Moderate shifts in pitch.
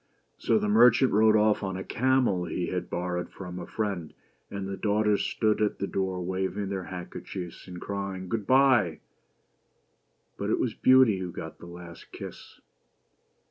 Yes: average, 3.2 semitones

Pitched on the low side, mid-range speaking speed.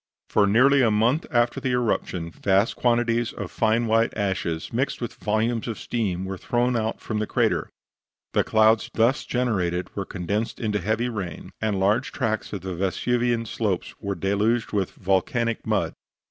Yes: low, 110 Hz; average, 165 wpm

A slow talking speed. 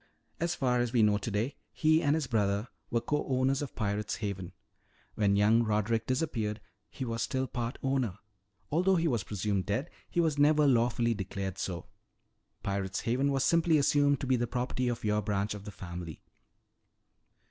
No: average, 175 wpm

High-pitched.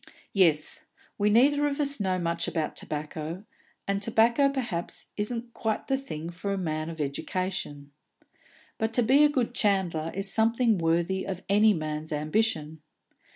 Yes: high, 195 Hz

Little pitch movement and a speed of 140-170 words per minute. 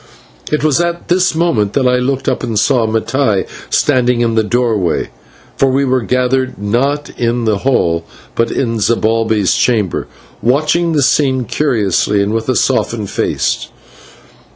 No: average, 3.6 semitones; average, 155 wpm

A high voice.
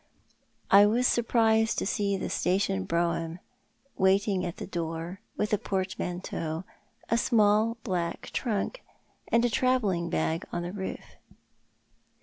Yes: high, 195 Hz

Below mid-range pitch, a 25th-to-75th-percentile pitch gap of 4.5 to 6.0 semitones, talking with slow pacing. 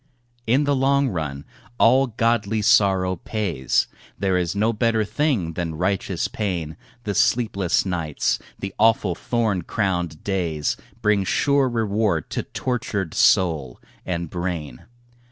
Yes: very low, 95 Hz; average, 4.8 semitones; slow, 125 wpm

